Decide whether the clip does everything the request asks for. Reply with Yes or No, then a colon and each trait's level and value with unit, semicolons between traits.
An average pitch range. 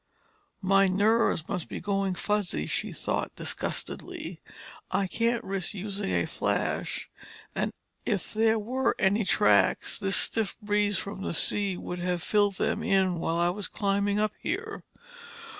No: narrow, 2.1 semitones